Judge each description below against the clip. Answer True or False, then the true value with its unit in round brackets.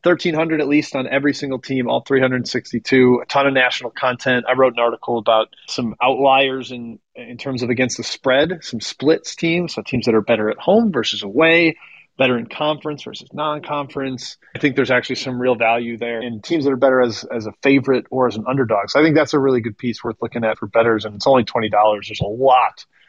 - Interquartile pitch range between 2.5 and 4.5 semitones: True (3.1 semitones)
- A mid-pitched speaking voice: False (130 Hz)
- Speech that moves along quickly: True (225 wpm)